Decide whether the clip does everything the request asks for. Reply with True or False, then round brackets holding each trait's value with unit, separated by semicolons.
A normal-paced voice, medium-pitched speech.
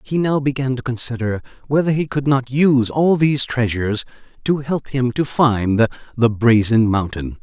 False (170 wpm; 130 Hz)